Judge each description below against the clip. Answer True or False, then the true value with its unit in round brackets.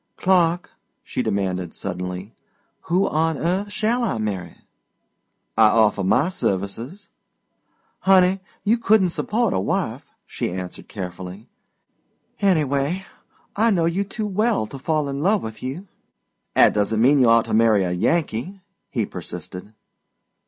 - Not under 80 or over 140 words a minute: True (135 wpm)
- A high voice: False (140 Hz)